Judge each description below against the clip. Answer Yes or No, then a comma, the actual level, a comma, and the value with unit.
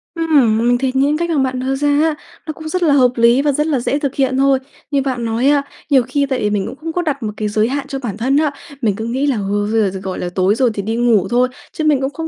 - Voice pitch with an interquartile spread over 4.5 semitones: No, average, 4.2 semitones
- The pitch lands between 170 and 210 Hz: No, very high, 265 Hz